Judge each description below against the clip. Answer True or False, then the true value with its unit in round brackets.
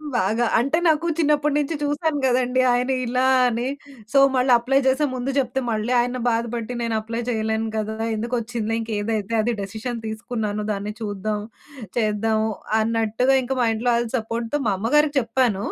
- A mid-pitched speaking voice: False (235 Hz)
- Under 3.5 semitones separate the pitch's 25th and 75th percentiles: True (2.8 semitones)